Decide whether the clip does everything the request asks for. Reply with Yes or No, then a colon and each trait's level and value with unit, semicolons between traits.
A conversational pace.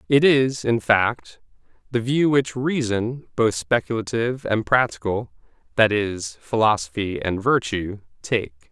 No: slow, 125 wpm